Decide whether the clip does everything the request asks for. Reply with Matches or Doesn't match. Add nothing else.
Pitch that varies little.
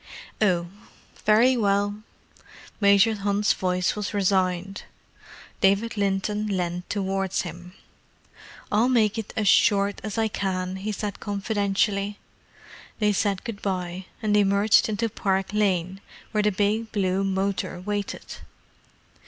Matches